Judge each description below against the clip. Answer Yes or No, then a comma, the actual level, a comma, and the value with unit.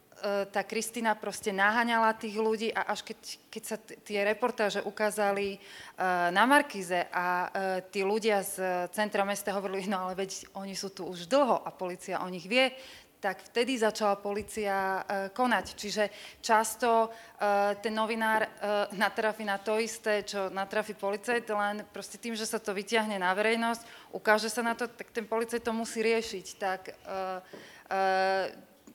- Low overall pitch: No, high, 205 Hz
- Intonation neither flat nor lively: No, narrow, 2.3 semitones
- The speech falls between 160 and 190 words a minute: Yes, fast, 165 wpm